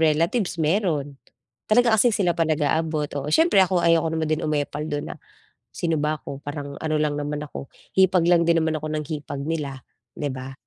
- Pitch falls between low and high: Yes, medium, 155 Hz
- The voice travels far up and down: No, narrow, 2.3 semitones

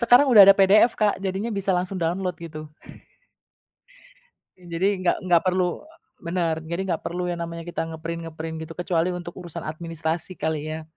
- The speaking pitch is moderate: Yes, medium, 175 Hz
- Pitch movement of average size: No, narrow, 2.2 semitones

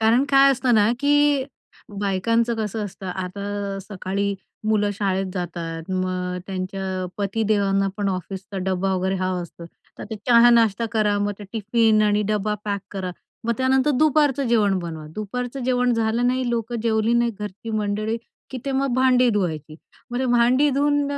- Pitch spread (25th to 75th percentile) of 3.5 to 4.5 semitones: Yes, average, 3.9 semitones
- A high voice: Yes, high, 210 Hz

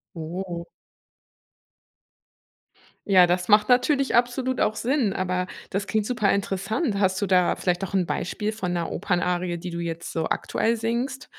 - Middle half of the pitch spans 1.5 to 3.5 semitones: No, average, 4.2 semitones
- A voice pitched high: Yes, high, 195 Hz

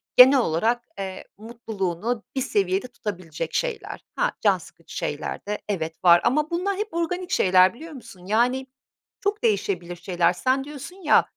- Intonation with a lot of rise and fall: Yes, wide, 7.4 semitones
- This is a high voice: Yes, high, 230 Hz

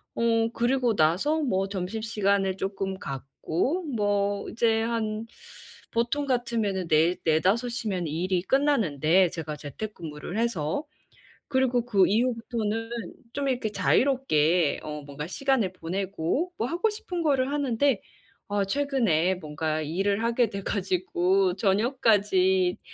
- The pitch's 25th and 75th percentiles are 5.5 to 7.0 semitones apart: No, average, 5.1 semitones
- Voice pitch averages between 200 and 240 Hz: Yes, high, 205 Hz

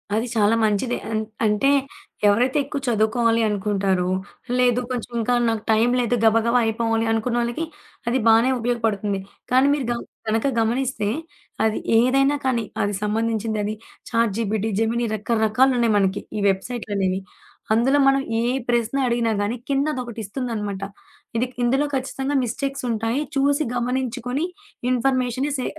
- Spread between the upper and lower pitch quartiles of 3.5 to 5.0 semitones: No, average, 2.7 semitones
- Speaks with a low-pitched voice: No, high, 230 Hz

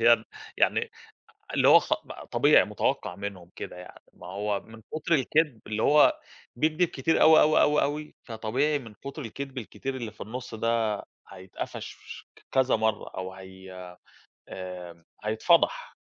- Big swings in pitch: Yes, wide, 5.8 semitones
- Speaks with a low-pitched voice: Yes, low, 115 Hz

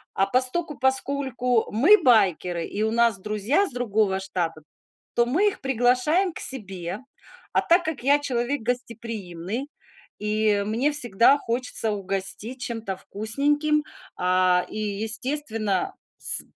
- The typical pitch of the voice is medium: No, high, 230 Hz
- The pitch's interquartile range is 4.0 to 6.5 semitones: Yes, average, 4.9 semitones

